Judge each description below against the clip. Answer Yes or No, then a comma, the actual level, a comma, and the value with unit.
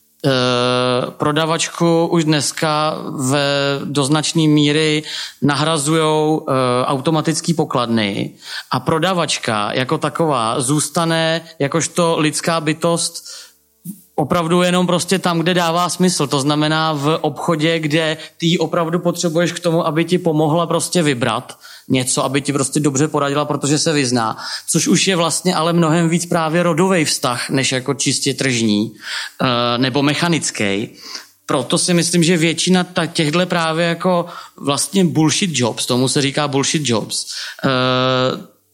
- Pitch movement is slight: No, average, 3.3 semitones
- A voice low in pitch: No, medium, 155 Hz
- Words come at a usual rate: Yes, average, 125 wpm